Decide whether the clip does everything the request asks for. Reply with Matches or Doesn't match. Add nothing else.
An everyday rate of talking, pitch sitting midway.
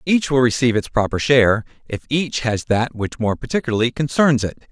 Doesn't match